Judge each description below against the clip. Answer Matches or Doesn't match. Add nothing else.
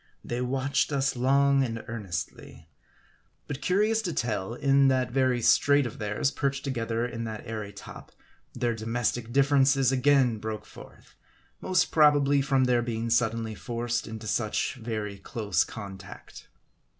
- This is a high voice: Doesn't match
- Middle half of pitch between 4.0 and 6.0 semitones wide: Doesn't match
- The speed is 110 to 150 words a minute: Matches